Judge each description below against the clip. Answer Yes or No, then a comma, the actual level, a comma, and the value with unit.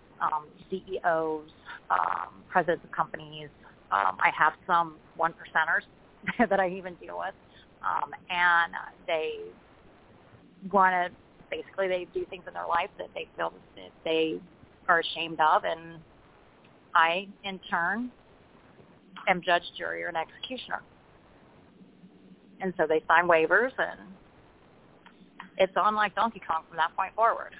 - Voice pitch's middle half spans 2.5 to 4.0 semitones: Yes, average, 3.3 semitones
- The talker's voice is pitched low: No, medium, 180 Hz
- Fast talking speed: No, slow, 135 wpm